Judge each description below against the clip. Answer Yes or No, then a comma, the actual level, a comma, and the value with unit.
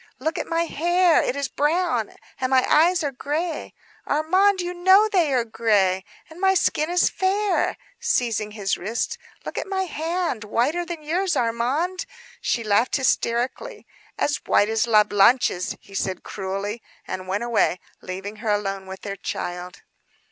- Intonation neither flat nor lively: No, wide, 8.8 semitones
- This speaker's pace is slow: No, average, 160 wpm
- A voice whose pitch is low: No, very high, 260 Hz